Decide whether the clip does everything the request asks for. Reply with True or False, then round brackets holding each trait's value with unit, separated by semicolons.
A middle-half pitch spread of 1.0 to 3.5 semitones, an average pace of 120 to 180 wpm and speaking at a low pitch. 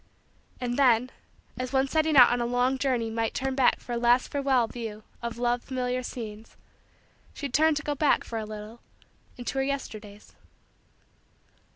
False (2.6 semitones; 170 wpm; 245 Hz)